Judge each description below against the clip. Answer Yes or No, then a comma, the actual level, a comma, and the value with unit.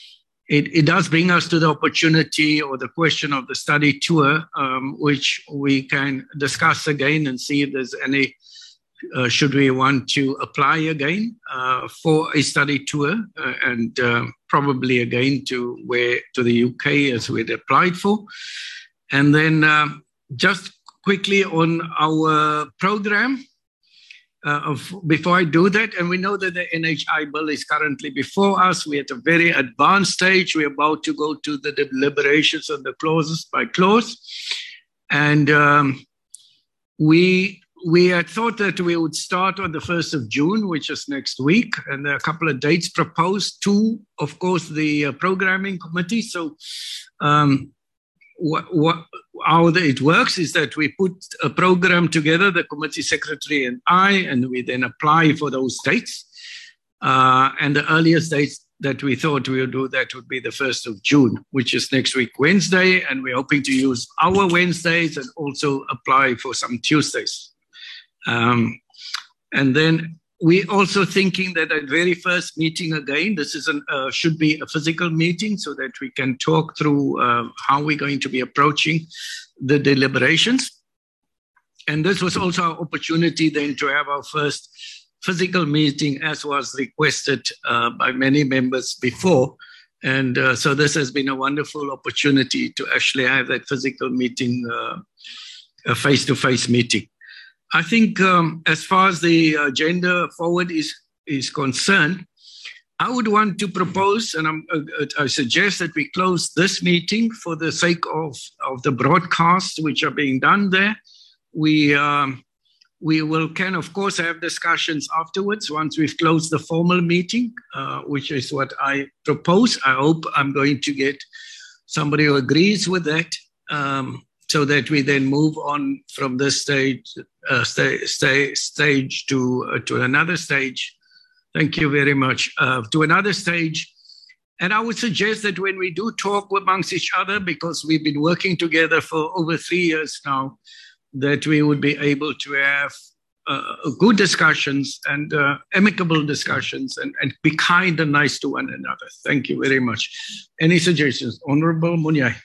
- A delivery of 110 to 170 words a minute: Yes, average, 165 wpm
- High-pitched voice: No, medium, 155 Hz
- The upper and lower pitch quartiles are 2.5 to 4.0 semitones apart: No, average, 4.4 semitones